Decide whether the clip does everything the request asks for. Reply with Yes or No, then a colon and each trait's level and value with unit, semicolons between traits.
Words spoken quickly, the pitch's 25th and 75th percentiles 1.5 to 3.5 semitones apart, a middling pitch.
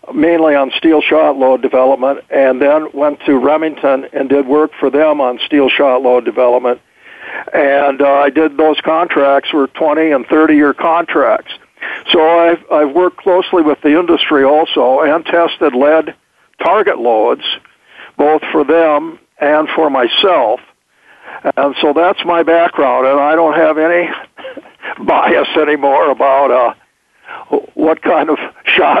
No: average, 145 wpm; narrow, 2.4 semitones; medium, 150 Hz